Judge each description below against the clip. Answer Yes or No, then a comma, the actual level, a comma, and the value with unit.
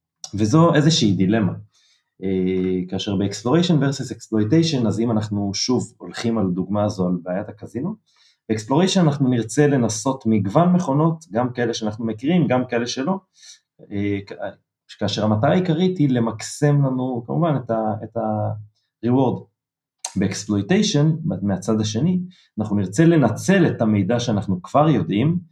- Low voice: Yes, low, 115 Hz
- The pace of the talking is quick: No, average, 130 wpm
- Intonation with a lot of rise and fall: Yes, wide, 6.4 semitones